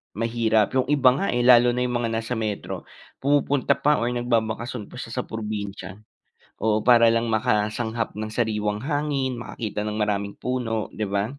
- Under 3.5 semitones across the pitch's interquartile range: Yes, average, 2.7 semitones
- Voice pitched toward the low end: Yes, low, 115 Hz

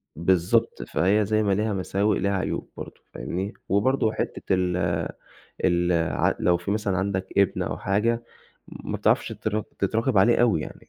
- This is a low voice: Yes, low, 100 Hz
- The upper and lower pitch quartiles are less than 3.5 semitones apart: Yes, average, 2.8 semitones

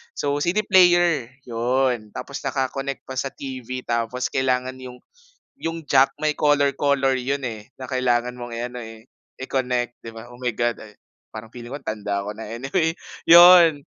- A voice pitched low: Yes, low, 130 Hz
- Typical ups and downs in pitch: Yes, average, 3.0 semitones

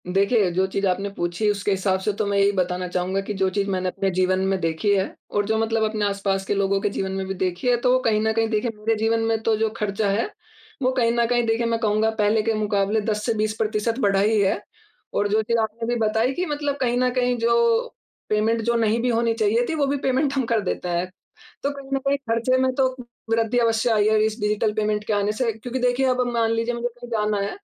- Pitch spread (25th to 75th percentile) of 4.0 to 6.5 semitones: No, average, 2.8 semitones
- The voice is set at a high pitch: Yes, high, 220 Hz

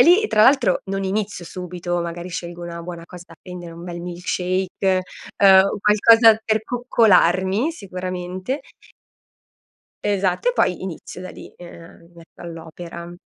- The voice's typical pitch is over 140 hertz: Yes, medium, 185 Hz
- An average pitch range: Yes, average, 3.0 semitones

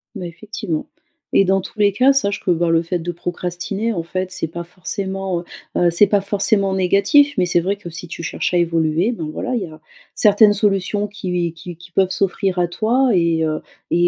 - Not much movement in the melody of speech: No, average, 3.0 semitones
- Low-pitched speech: No, medium, 185 Hz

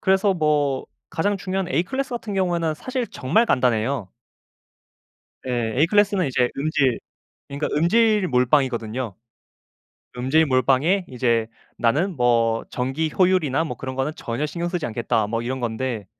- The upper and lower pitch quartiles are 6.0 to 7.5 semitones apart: Yes, wide, 6.5 semitones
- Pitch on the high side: No, medium, 140 Hz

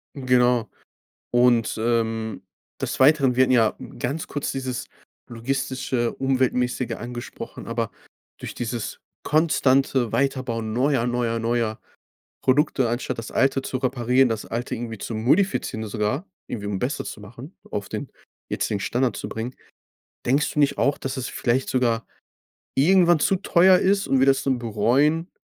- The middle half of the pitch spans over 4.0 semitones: No, average, 2.8 semitones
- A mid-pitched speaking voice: No, low, 125 Hz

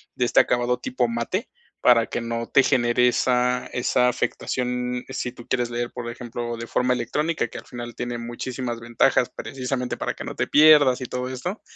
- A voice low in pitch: Yes, low, 125 Hz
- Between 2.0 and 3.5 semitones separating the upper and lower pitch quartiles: No, narrow, 1.1 semitones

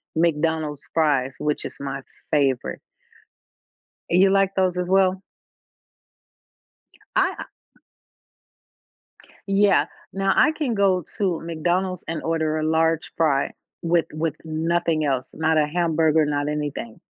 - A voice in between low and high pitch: Yes, medium, 160 Hz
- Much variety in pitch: No, average, 3.3 semitones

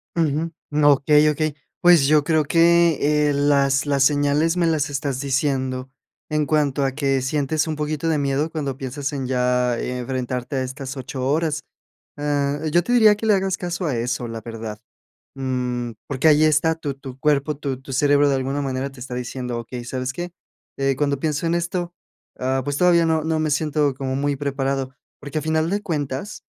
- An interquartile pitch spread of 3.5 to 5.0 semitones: No, average, 2.8 semitones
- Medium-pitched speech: Yes, medium, 145 Hz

